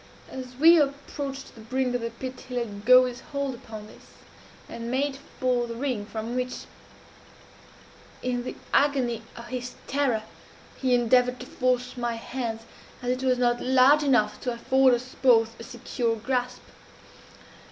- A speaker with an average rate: Yes, average, 160 wpm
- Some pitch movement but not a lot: No, narrow, 1.9 semitones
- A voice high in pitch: Yes, very high, 250 Hz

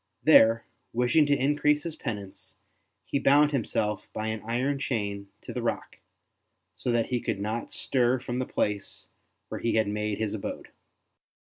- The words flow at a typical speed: Yes, average, 160 wpm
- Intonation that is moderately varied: Yes, average, 4.2 semitones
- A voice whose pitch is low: Yes, low, 115 Hz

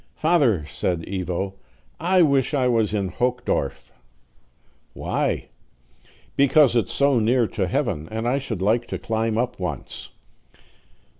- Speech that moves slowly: Yes, slow, 130 wpm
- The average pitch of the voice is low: Yes, low, 115 Hz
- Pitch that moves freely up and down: Yes, wide, 5.7 semitones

